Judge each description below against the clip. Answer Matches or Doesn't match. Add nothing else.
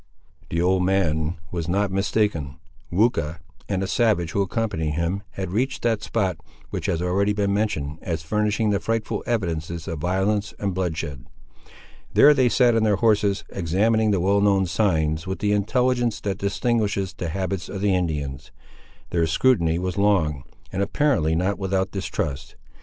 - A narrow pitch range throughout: Doesn't match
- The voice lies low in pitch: Matches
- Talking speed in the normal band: Matches